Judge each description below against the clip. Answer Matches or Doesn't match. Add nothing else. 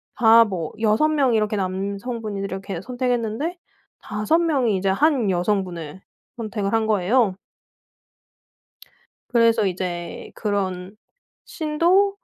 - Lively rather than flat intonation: Doesn't match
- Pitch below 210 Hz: Doesn't match